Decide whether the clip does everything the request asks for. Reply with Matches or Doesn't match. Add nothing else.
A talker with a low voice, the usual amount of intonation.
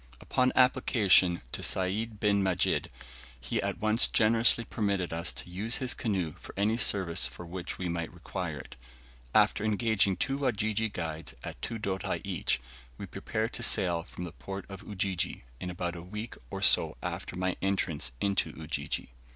Matches